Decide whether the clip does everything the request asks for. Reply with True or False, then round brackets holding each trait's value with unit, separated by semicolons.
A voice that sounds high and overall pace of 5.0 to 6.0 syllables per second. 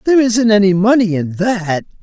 True (205 Hz; 5.2 syllables/s)